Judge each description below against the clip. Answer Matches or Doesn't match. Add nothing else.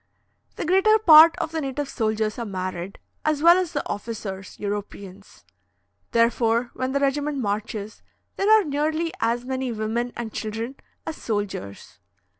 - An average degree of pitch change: Doesn't match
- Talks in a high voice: Matches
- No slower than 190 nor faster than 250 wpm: Doesn't match